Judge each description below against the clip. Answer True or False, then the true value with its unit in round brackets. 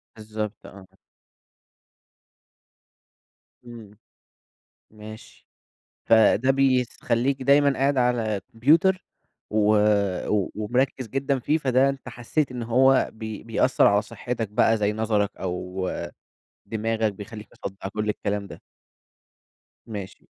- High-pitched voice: False (115 Hz)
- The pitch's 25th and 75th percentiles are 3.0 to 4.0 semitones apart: True (3.6 semitones)